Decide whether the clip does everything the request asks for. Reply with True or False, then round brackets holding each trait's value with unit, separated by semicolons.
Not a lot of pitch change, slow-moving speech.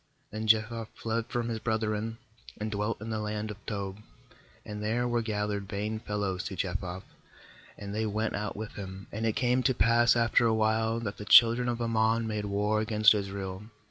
False (1.7 semitones; 200 wpm)